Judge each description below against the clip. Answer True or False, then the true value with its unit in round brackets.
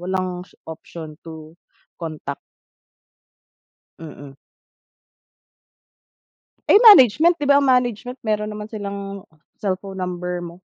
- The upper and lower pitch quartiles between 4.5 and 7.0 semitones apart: True (4.8 semitones)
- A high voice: True (195 Hz)